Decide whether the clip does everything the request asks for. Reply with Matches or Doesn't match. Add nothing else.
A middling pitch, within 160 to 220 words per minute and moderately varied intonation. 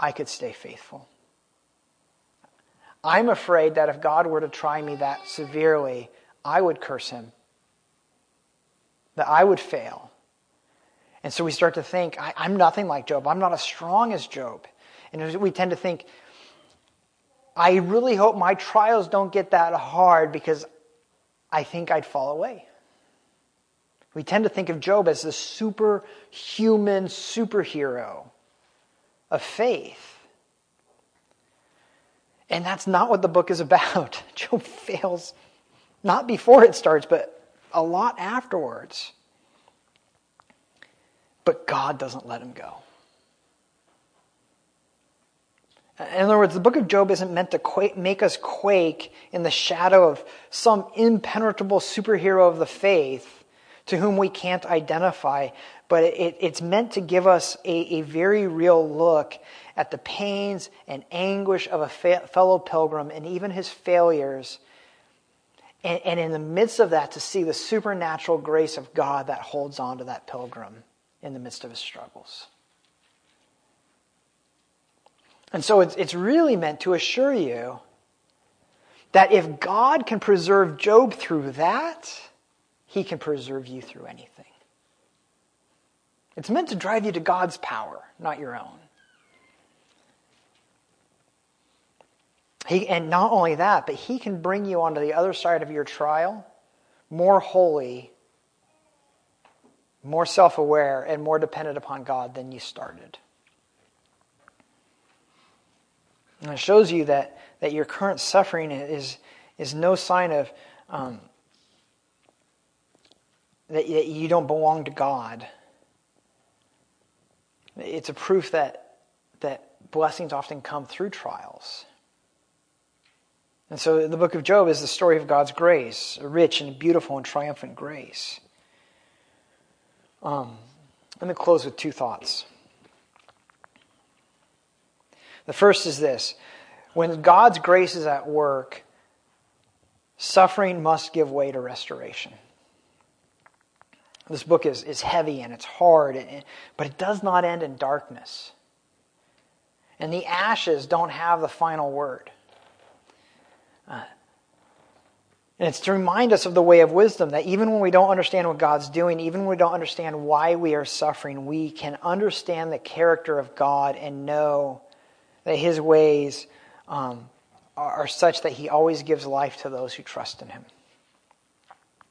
Doesn't match